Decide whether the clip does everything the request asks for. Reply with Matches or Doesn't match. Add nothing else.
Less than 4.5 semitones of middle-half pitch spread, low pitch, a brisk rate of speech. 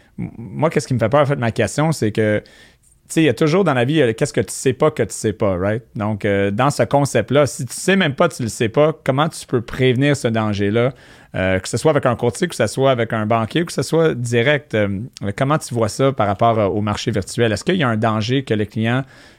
Doesn't match